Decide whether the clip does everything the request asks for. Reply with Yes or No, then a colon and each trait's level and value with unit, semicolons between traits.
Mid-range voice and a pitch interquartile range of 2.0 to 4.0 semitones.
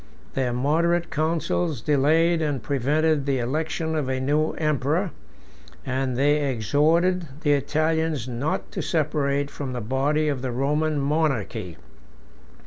Yes: medium, 145 Hz; average, 3.0 semitones